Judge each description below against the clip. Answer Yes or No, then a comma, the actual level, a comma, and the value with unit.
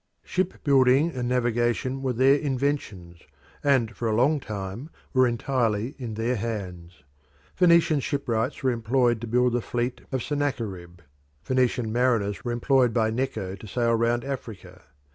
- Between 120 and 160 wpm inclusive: Yes, average, 145 wpm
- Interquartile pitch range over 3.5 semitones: No, average, 3.2 semitones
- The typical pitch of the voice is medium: No, low, 120 Hz